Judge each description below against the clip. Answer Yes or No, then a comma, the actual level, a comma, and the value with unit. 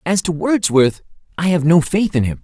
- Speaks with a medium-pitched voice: Yes, medium, 165 Hz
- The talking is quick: Yes, fast, 220 wpm